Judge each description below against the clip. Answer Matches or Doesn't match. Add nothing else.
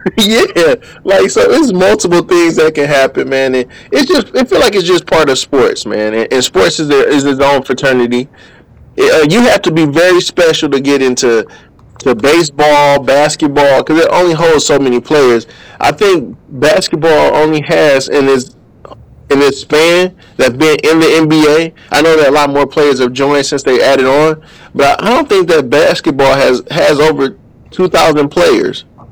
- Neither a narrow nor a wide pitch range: Matches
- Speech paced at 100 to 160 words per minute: Doesn't match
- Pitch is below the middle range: Doesn't match